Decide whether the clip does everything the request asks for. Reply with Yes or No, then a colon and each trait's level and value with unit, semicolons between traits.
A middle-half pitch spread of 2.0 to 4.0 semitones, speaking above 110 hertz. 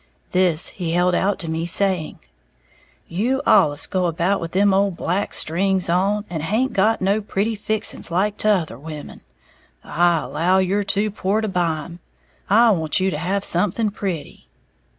Yes: average, 3.2 semitones; medium, 185 Hz